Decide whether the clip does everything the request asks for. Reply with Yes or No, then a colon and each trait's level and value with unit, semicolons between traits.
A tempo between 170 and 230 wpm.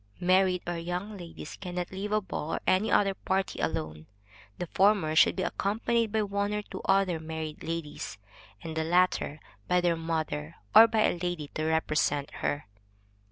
Yes: average, 175 wpm